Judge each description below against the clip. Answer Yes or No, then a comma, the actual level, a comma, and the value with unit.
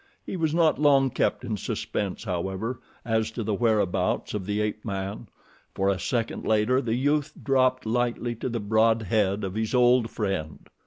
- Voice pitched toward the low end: Yes, low, 110 Hz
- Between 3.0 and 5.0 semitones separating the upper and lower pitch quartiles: Yes, average, 3.6 semitones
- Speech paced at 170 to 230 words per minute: Yes, average, 175 wpm